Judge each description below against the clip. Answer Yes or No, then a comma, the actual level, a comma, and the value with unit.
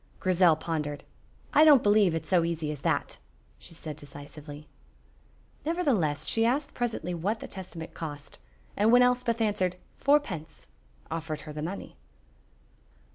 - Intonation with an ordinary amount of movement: No, wide, 6.7 semitones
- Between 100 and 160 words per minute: Yes, average, 140 wpm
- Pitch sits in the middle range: Yes, medium, 175 Hz